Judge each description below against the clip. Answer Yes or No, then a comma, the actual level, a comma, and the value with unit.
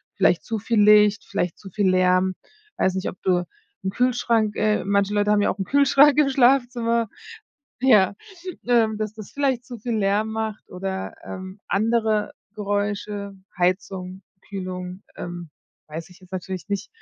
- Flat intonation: No, average, 3.1 semitones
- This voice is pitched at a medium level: No, high, 205 Hz